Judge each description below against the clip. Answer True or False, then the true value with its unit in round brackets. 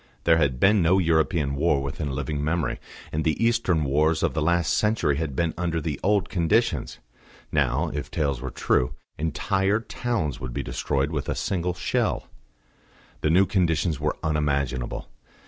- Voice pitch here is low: True (80 Hz)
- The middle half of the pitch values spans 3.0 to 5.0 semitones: True (3.5 semitones)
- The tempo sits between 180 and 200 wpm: False (165 wpm)